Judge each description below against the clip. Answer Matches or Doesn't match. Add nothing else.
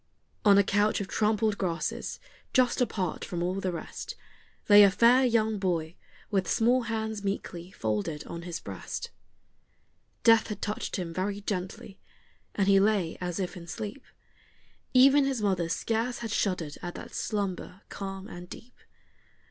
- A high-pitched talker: Matches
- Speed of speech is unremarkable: Matches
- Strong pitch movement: Doesn't match